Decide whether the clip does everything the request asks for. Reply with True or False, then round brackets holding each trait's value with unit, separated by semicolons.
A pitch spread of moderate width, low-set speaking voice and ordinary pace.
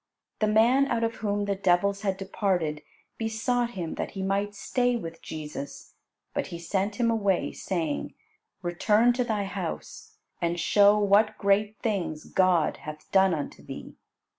False (3.8 semitones; 200 Hz; 155 wpm)